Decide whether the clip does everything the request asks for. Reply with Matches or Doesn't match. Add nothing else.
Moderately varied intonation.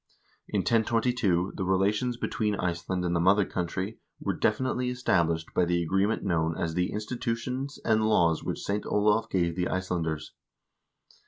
Matches